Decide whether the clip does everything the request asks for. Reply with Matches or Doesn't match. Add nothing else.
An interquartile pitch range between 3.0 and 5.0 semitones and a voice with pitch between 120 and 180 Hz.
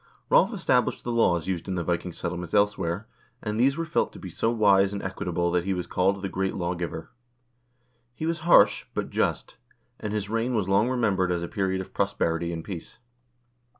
Doesn't match